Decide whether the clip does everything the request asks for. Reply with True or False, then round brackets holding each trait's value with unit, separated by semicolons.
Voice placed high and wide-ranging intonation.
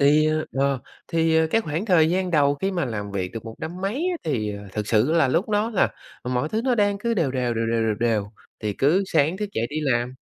False (150 Hz; 7.6 semitones)